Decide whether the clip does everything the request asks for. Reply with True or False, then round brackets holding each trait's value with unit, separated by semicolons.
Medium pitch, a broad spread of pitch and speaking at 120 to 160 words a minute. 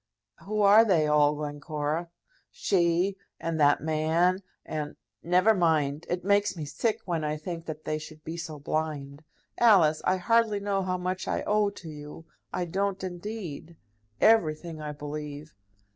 False (165 Hz; 3.8 semitones; 155 wpm)